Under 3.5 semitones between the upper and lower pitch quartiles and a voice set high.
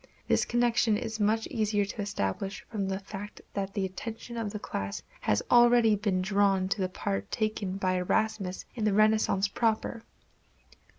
Yes: narrow, 2.4 semitones; high, 205 Hz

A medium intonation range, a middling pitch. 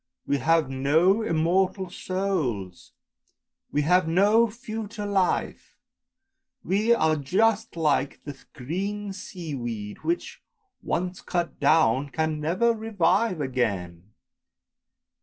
No: wide, 6.1 semitones; medium, 170 Hz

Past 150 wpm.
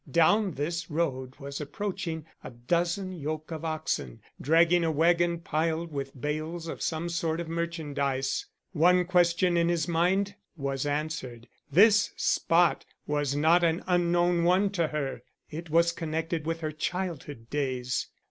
No: average, 145 wpm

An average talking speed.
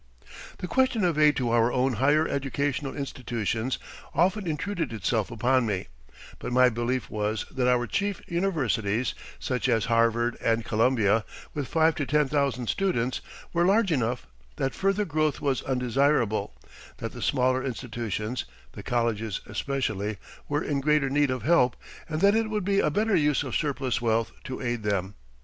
Yes: average, 165 wpm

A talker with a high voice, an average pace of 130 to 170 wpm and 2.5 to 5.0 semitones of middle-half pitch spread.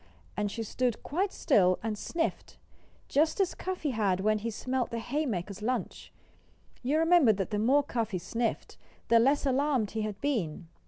No: high, 235 Hz; average, 165 wpm; wide, 5.4 semitones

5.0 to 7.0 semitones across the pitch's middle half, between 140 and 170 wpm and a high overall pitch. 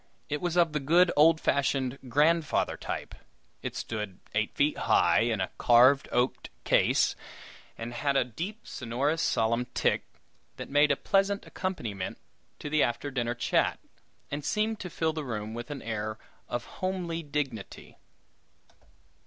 No: wide, 5.5 semitones; average, 150 wpm; medium, 140 Hz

